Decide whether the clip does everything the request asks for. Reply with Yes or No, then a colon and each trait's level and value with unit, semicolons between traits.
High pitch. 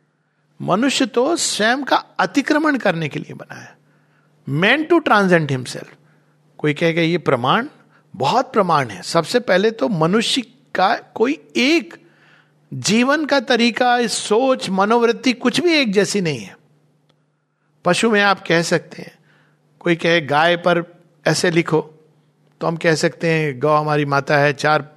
No: medium, 175 Hz